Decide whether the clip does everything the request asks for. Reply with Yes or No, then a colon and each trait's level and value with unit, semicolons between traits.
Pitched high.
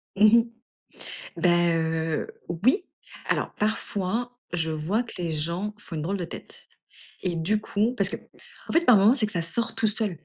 Yes: high, 200 Hz